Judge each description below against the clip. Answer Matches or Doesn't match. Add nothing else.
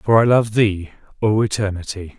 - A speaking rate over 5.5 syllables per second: Doesn't match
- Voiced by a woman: Doesn't match